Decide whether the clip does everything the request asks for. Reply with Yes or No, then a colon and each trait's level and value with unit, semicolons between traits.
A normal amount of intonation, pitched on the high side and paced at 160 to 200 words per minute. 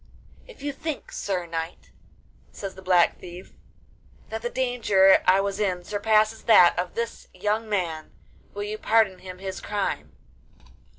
No: average, 3.3 semitones; high, 200 Hz; average, 145 wpm